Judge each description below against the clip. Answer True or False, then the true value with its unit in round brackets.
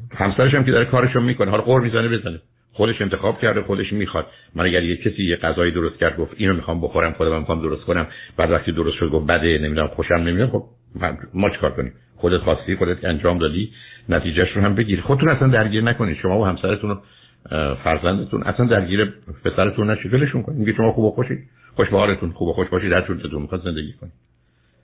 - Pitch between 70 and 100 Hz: True (95 Hz)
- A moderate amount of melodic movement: True (4.7 semitones)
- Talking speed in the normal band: False (205 wpm)